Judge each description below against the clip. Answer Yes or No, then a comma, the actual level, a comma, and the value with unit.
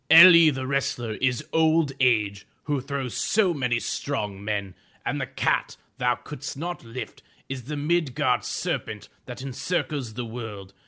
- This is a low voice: Yes, low, 130 Hz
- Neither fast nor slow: Yes, average, 150 wpm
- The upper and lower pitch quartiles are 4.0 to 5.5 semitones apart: Yes, average, 4.5 semitones